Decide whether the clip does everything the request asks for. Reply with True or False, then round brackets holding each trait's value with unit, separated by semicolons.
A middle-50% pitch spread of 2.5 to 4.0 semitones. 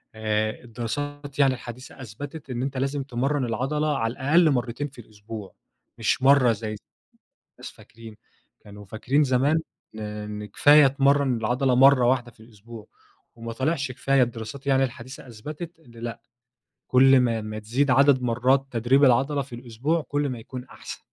True (3.3 semitones)